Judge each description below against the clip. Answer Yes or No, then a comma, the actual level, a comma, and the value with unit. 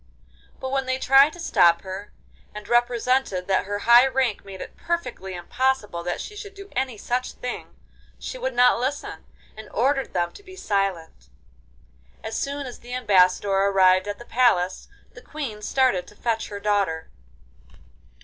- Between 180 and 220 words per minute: No, average, 165 wpm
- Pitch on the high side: Yes, high, 230 Hz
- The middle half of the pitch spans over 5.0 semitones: Yes, wide, 5.5 semitones